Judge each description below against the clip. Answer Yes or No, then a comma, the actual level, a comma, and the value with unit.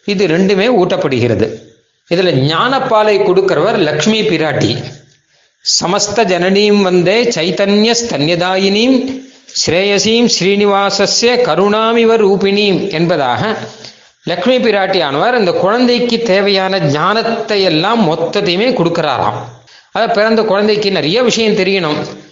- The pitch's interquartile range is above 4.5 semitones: No, average, 3.8 semitones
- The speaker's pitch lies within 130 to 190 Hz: No, high, 200 Hz